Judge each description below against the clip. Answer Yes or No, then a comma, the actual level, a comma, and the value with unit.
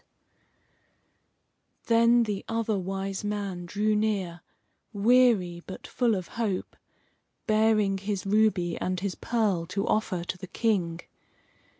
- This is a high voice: Yes, high, 200 Hz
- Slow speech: Yes, slow, 115 wpm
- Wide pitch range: No, average, 3.0 semitones